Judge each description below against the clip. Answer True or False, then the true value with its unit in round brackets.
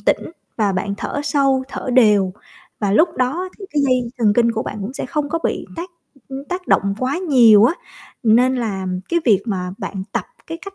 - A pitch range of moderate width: False (5.7 semitones)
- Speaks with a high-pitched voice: True (255 Hz)